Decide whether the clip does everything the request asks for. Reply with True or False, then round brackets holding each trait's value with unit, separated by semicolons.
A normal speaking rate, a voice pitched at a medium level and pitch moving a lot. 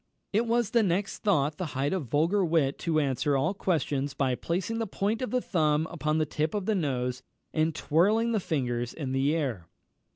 True (195 wpm; 160 Hz; 5.9 semitones)